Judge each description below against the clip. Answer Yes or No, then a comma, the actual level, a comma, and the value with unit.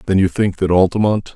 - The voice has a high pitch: No, very low, 95 Hz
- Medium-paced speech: No, fast, 220 wpm